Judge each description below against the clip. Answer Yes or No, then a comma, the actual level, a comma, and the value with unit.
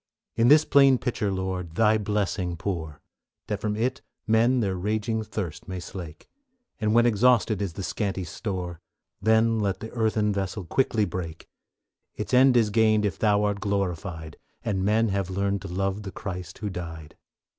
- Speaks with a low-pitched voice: Yes, low, 100 Hz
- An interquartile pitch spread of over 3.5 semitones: No, average, 3.2 semitones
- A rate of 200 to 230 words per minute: No, average, 165 wpm